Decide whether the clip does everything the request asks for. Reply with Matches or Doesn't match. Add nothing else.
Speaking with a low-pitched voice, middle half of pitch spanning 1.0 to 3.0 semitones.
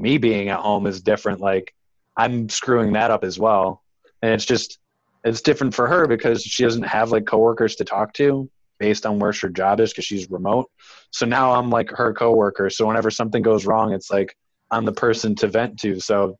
Matches